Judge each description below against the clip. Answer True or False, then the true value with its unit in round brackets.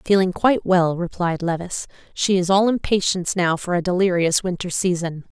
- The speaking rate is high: False (165 wpm)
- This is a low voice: False (180 Hz)